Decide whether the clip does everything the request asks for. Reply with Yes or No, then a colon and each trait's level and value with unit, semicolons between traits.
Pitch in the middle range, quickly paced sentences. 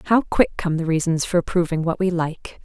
Yes: medium, 170 Hz; fast, 225 wpm